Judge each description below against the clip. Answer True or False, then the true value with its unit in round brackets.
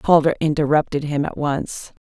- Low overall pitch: False (150 Hz)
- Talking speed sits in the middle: True (150 wpm)